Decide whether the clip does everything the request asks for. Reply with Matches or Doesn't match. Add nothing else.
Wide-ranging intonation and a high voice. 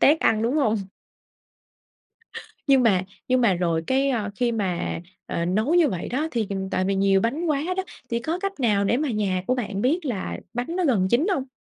Matches